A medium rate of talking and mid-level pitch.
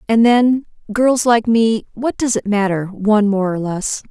No: average, 190 wpm; high, 220 Hz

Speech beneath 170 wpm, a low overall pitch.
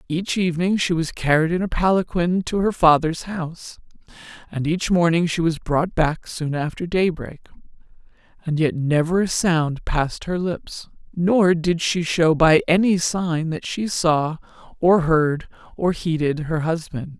No: average, 160 wpm; medium, 165 Hz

